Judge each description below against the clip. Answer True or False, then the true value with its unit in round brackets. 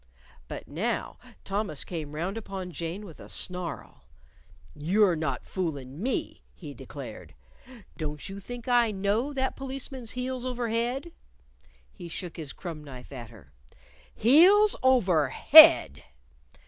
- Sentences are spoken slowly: True (130 wpm)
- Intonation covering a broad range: True (8.3 semitones)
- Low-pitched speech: False (190 Hz)